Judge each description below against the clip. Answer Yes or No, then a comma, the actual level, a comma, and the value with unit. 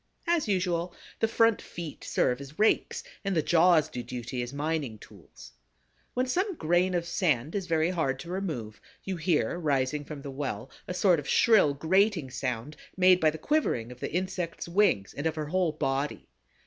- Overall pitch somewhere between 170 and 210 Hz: No, medium, 160 Hz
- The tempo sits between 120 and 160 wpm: No, average, 185 wpm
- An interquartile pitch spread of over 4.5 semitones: Yes, average, 5.2 semitones